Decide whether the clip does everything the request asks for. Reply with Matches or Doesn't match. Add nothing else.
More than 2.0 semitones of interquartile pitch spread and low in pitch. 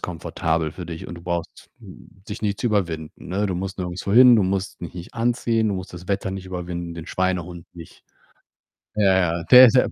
Matches